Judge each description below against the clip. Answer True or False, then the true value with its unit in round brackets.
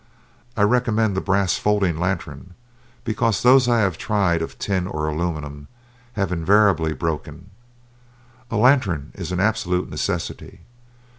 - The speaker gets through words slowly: True (130 wpm)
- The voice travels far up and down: False (4.6 semitones)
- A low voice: True (95 Hz)